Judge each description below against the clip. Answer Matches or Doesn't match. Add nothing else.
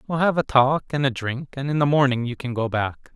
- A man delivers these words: Matches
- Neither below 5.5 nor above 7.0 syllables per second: Matches